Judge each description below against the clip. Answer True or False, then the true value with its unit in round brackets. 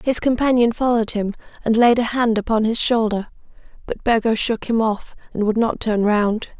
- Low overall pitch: False (225 Hz)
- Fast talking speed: False (190 wpm)